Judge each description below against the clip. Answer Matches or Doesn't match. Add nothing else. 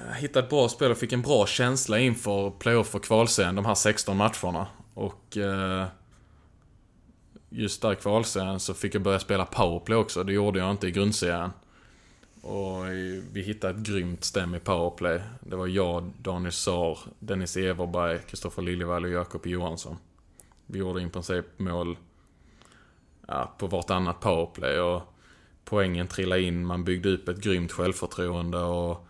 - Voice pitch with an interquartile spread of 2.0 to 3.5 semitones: Matches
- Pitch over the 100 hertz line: Doesn't match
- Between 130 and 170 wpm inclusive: Matches